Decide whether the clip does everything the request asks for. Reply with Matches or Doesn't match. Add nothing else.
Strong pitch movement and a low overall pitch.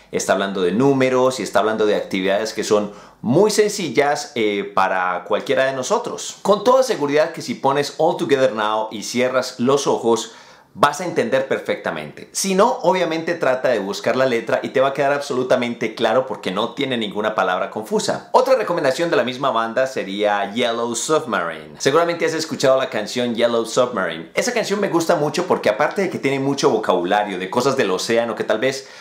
Matches